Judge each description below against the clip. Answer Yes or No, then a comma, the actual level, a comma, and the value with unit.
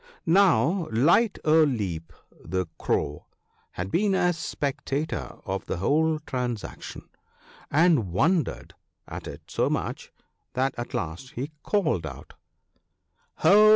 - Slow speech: Yes, slow, 120 wpm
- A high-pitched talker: No, medium, 140 Hz